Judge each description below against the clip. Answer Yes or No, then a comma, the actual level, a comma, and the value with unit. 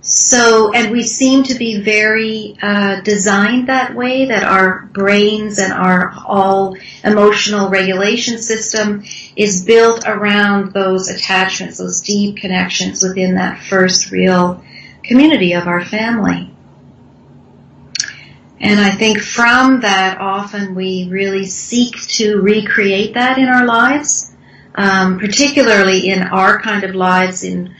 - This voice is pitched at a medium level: No, high, 205 Hz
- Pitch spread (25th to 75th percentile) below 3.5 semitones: Yes, average, 2.9 semitones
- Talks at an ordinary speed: No, slow, 125 wpm